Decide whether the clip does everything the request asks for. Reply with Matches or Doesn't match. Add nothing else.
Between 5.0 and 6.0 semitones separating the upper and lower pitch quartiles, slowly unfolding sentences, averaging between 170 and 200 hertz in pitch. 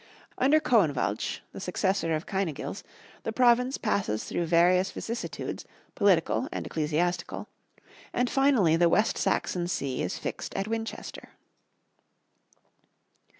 Matches